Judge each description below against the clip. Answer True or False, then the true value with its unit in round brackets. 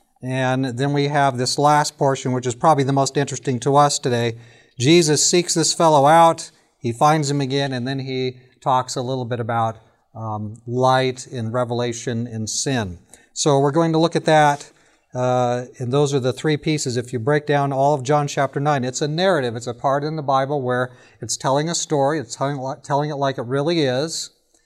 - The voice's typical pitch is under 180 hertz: True (135 Hz)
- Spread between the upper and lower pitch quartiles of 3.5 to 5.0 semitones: False (3.0 semitones)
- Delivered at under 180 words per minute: False (205 wpm)